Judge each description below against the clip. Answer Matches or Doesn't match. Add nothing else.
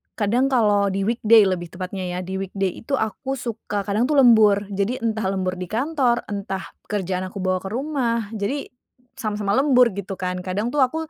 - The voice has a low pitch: Doesn't match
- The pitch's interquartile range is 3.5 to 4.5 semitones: Matches